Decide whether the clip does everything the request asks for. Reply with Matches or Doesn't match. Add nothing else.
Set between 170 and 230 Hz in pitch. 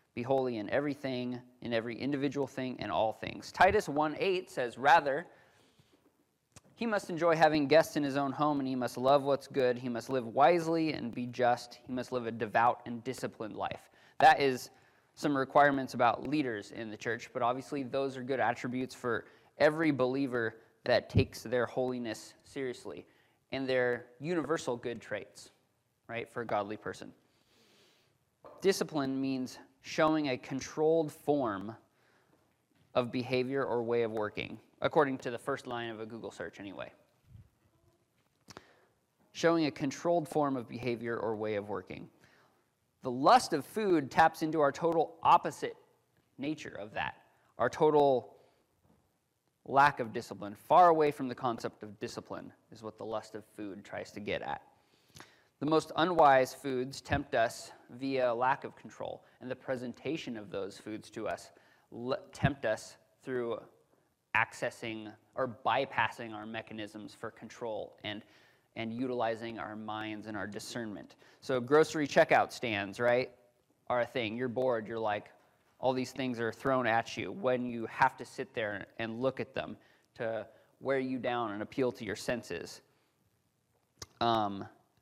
Doesn't match